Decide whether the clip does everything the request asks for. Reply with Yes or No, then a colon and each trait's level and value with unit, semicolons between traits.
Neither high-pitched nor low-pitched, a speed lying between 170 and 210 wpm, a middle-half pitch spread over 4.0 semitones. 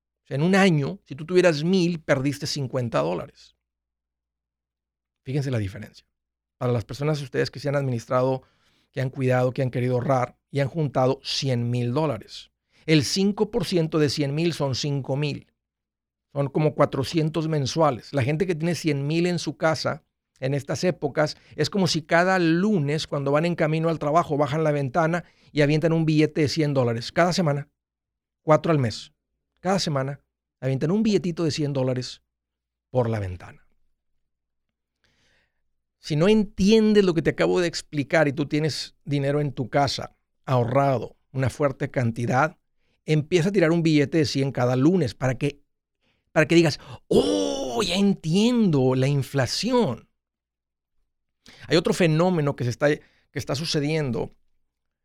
No: medium, 145 Hz; average, 155 wpm; average, 4.4 semitones